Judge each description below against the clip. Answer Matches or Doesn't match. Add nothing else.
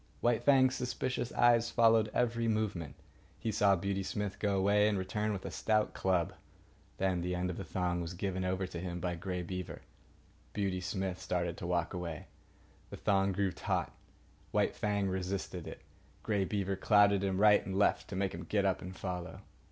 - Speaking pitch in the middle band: Doesn't match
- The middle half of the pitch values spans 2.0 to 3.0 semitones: Matches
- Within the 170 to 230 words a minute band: Matches